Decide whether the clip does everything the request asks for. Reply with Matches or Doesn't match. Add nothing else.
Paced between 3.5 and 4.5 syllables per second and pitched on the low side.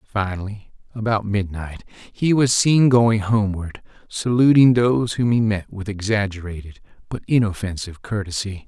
Doesn't match